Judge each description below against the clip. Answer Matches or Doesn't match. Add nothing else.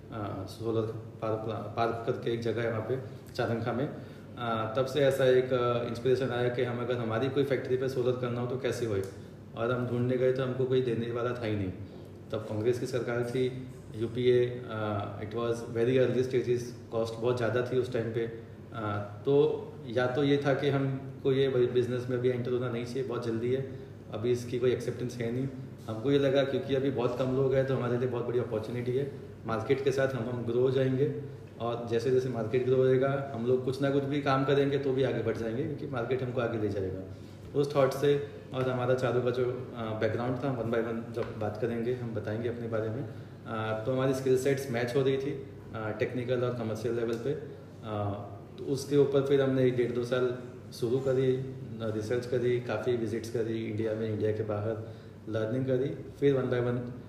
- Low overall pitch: Matches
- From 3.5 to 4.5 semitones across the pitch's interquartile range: Doesn't match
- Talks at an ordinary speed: Doesn't match